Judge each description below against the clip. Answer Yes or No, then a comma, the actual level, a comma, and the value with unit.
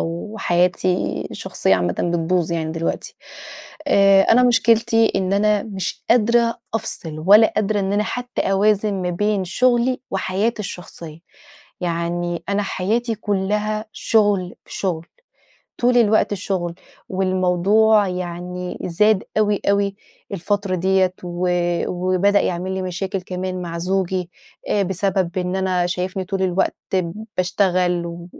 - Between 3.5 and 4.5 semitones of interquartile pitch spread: No, average, 2.7 semitones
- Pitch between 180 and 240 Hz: Yes, high, 190 Hz